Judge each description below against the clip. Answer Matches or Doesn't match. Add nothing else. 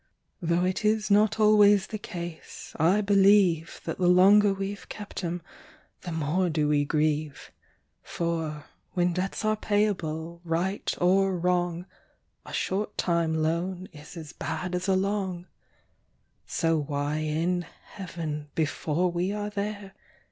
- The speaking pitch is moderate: Matches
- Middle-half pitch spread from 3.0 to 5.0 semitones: Matches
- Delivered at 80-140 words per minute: Matches